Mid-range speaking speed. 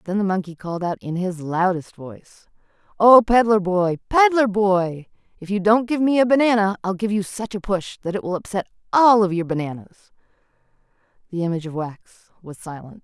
Yes: average, 190 wpm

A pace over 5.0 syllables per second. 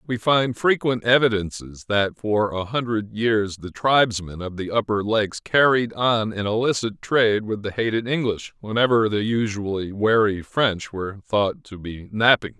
No: 4.6 syllables/s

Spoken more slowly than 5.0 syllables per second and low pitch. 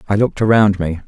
No: 7.0 syllables/s; low, 100 Hz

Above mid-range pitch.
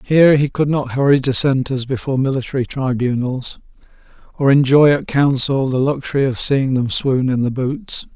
No: low, 135 Hz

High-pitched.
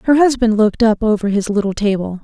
Yes: high, 215 Hz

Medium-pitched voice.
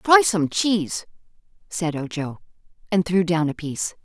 Yes: medium, 180 Hz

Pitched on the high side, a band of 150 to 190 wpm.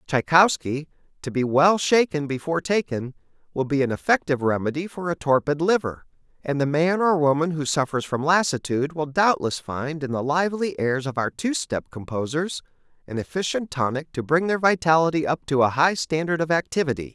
No: medium, 150 Hz; average, 180 wpm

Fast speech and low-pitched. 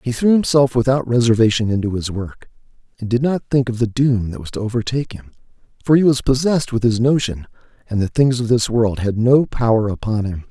Yes: fast, 215 wpm; low, 120 Hz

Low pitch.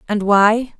No: high, 215 Hz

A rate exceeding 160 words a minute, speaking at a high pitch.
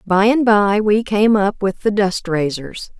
Yes: average, 200 wpm; high, 205 Hz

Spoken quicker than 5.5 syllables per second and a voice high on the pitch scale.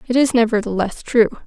Yes: 6.0 syllables/s; high, 230 Hz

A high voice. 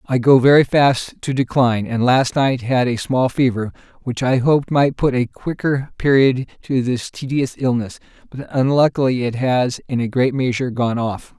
No: low, 130 Hz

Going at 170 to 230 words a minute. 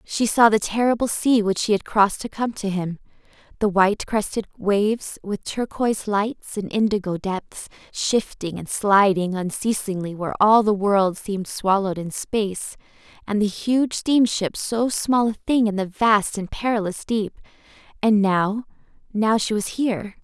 No: average, 155 wpm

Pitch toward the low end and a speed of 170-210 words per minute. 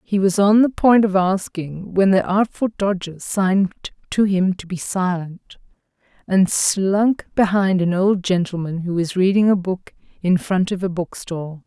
No: high, 190 Hz; average, 175 wpm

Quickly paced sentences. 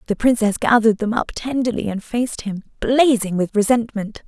No: average, 170 wpm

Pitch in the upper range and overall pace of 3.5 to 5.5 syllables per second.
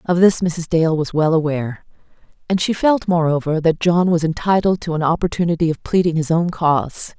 No: medium, 165 Hz; 5.4 syllables/s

